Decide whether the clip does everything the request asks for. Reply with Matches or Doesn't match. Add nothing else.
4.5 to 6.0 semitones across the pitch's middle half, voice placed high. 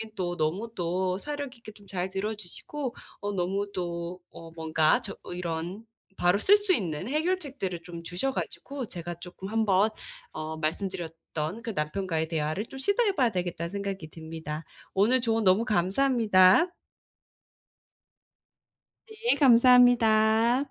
Matches